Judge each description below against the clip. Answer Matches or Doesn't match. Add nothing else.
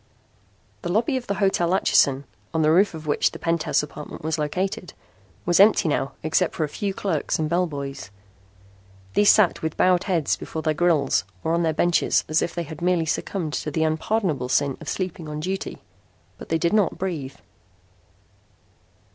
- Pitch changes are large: Doesn't match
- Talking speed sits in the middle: Matches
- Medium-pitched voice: Matches